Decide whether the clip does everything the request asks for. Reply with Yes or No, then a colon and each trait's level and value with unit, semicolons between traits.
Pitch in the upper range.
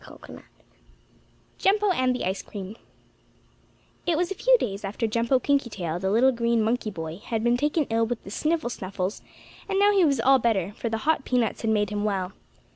Yes: high, 230 Hz